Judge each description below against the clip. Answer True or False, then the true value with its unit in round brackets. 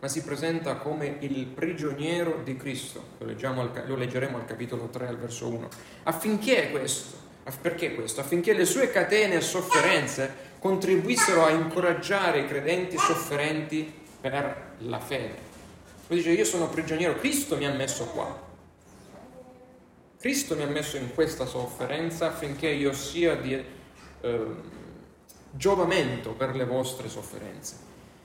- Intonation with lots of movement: False (4.2 semitones)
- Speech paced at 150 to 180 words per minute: False (135 wpm)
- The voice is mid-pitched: True (145 Hz)